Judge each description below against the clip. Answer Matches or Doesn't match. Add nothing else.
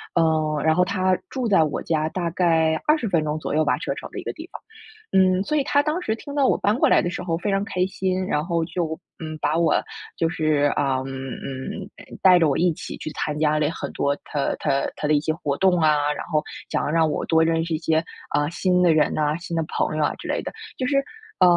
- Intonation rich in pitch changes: Doesn't match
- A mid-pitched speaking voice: Matches